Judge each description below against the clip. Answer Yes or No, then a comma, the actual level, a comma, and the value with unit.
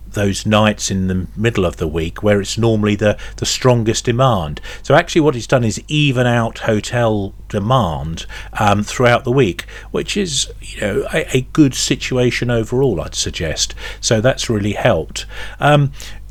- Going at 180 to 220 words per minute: No, average, 165 wpm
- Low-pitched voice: Yes, low, 110 Hz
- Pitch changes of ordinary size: Yes, average, 4.0 semitones